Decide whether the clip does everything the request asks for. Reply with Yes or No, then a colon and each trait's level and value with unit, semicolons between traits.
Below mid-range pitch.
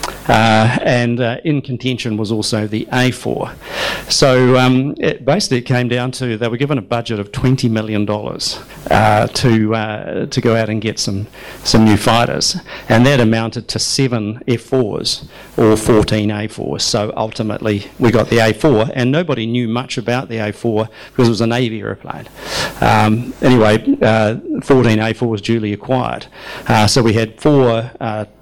Yes: low, 115 Hz